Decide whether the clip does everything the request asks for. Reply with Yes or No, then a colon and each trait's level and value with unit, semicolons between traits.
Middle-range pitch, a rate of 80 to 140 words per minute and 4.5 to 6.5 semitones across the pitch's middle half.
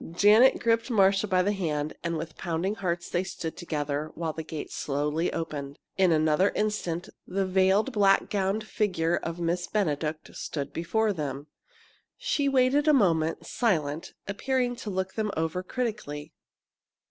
No: medium, 180 Hz; average, 150 wpm; average, 4.8 semitones